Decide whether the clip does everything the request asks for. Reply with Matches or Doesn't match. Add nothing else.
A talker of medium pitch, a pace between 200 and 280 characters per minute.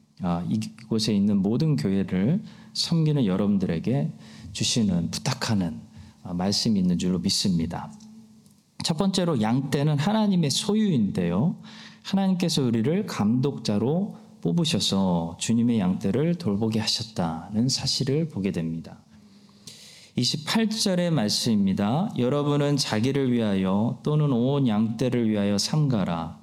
Matches